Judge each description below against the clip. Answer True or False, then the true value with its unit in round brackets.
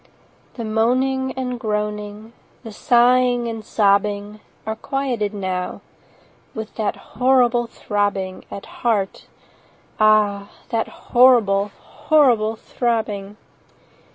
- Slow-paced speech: True (95 wpm)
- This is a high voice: True (220 Hz)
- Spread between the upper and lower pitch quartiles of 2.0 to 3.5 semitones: True (2.9 semitones)